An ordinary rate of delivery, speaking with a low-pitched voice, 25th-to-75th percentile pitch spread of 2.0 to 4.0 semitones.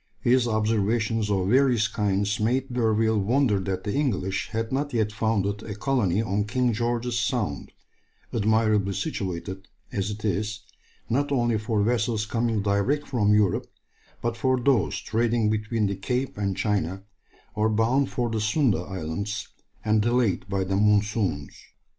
Yes: average, 145 wpm; low, 110 Hz; average, 2.7 semitones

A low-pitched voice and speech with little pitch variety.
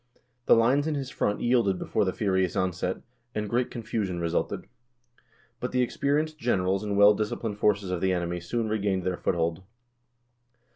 No: low, 105 Hz; average, 4.2 semitones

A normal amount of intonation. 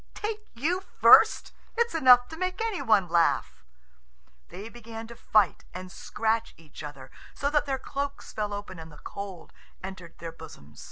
No: wide, 7.9 semitones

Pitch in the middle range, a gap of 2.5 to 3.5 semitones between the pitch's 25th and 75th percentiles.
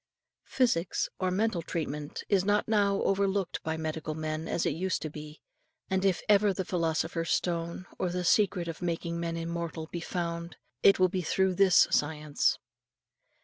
Yes: medium, 170 Hz; average, 2.8 semitones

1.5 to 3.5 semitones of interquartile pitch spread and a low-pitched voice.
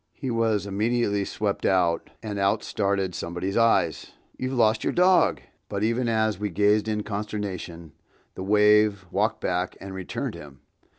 Yes: narrow, 2.5 semitones; low, 105 Hz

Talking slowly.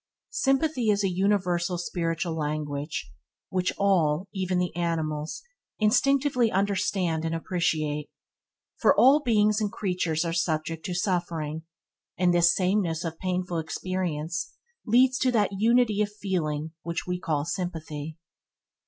Yes: slow, 125 wpm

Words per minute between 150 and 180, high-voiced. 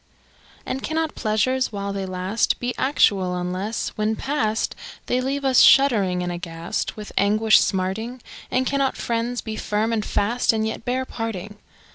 Yes: average, 160 wpm; high, 220 Hz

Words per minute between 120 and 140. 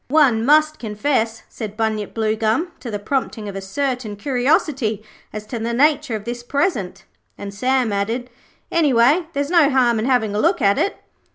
No: average, 175 wpm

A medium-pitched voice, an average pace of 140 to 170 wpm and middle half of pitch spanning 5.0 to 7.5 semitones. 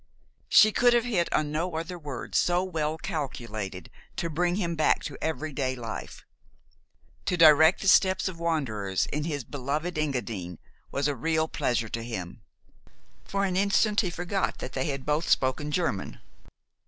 Yes: medium, 155 Hz; average, 165 wpm; wide, 5.4 semitones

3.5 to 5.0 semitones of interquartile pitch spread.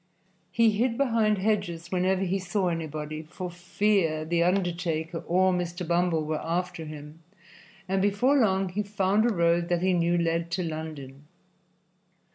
No: average, 2.8 semitones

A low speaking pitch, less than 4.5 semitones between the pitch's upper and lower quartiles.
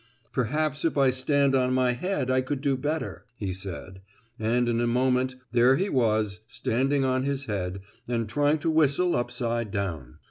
Yes: low, 130 Hz; average, 3.7 semitones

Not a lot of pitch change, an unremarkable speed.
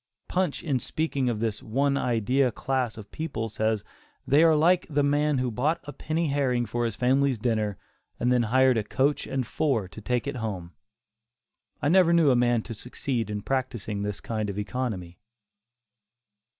No: average, 4.2 semitones; average, 175 wpm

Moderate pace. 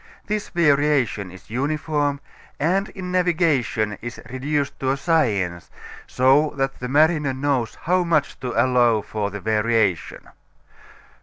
No: slow, 130 wpm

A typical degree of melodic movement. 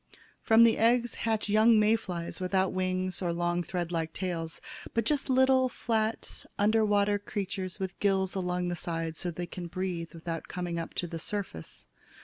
Yes: average, 3.7 semitones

